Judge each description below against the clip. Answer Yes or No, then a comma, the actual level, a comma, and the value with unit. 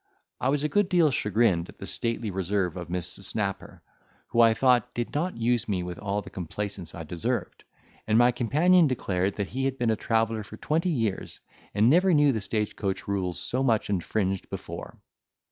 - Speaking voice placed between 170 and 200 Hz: No, low, 110 Hz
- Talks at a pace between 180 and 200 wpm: Yes, average, 195 wpm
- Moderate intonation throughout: Yes, average, 4.9 semitones